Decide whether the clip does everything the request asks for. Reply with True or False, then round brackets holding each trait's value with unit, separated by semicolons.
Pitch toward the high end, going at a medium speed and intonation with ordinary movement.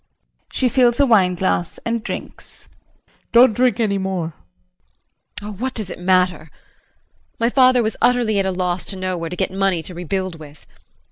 True (195 Hz; 185 wpm; 4.5 semitones)